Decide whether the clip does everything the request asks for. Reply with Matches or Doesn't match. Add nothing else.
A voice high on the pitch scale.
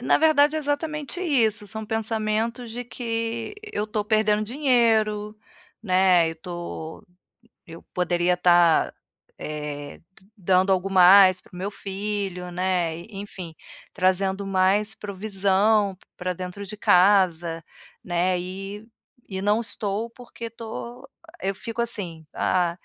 Matches